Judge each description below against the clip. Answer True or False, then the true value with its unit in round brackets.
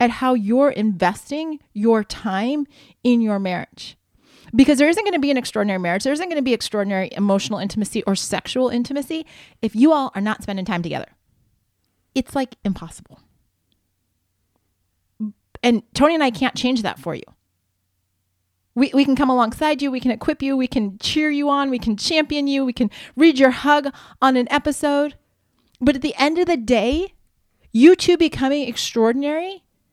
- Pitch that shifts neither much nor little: False (6.4 semitones)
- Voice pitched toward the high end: True (245 Hz)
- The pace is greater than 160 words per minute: True (170 wpm)